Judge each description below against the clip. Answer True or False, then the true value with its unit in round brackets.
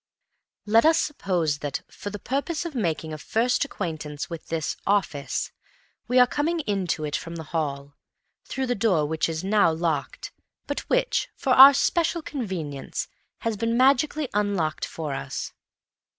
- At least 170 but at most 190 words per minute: False (155 wpm)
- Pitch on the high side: True (200 Hz)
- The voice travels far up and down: True (8.6 semitones)